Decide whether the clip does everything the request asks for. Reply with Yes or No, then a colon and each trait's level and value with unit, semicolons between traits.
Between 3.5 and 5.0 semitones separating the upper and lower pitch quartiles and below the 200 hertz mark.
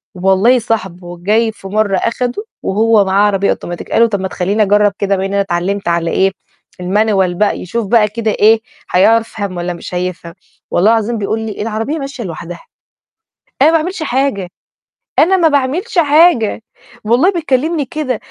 No: average, 4.4 semitones; high, 215 Hz